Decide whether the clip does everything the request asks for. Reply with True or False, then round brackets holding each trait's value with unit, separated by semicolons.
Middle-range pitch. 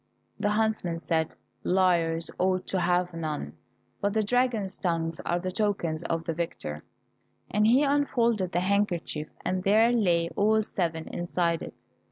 True (180 Hz)